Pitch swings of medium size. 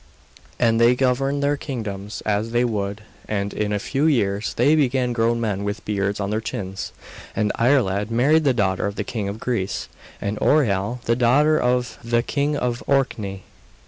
Yes: average, 3.8 semitones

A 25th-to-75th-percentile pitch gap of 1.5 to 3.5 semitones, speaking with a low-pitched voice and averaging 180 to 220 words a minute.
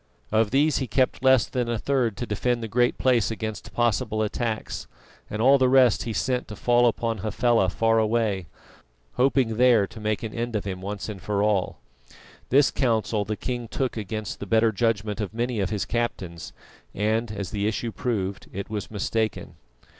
Yes: narrow, 2.6 semitones; low, 110 Hz; average, 185 wpm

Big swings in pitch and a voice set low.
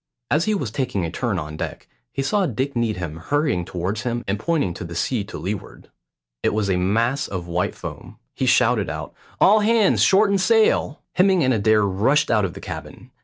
Yes: wide, 8.1 semitones; low, 115 Hz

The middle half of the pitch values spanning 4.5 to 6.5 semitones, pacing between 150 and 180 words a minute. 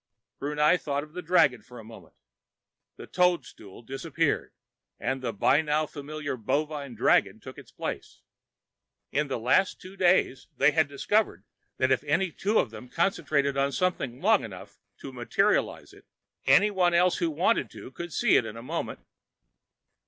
Yes: average, 4.8 semitones; average, 160 wpm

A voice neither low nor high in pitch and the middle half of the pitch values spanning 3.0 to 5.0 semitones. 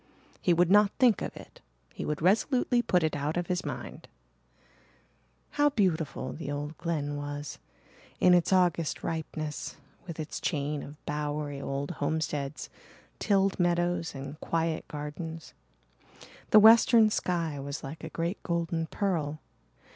Yes: medium, 165 Hz; average, 3.3 semitones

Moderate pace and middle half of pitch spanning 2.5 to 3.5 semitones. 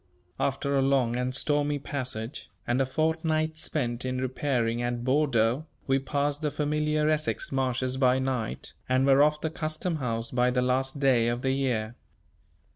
Yes: average, 165 wpm; average, 2.9 semitones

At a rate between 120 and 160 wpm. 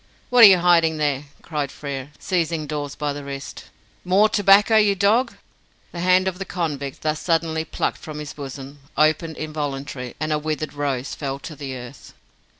No: average, 175 wpm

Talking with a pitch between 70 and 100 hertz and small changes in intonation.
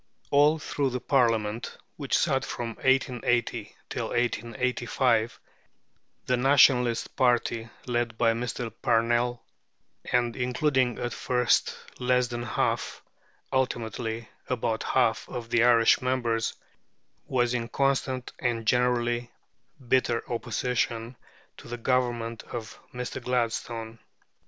No: low, 120 Hz; narrow, 1.5 semitones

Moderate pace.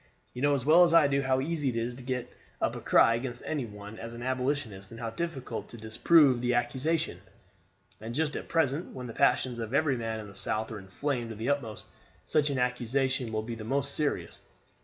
No: fast, 220 wpm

